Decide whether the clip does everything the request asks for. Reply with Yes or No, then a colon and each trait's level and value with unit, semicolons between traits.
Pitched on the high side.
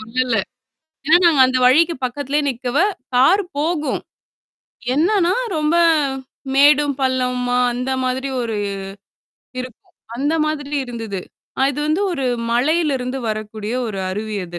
Yes: very high, 260 Hz